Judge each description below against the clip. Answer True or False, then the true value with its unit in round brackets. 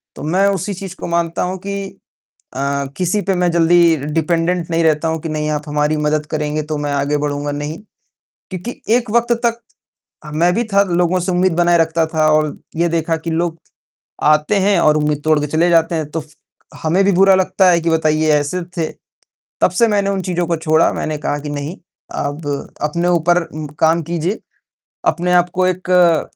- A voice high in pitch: False (165 Hz)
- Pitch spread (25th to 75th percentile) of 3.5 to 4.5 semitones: False (2.9 semitones)